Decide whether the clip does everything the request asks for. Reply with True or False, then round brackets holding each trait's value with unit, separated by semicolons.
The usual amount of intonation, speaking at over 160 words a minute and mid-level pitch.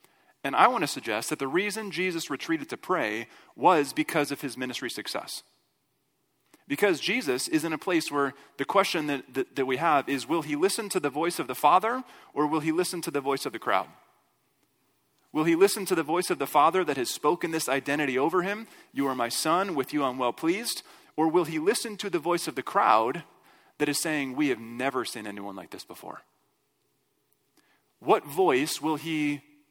True (4.2 semitones; 205 wpm; 150 Hz)